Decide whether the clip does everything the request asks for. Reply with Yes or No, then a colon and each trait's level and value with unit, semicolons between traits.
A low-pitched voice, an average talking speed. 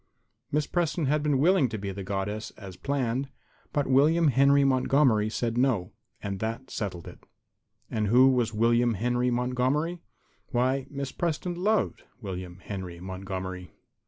Yes: low, 125 Hz; average, 145 wpm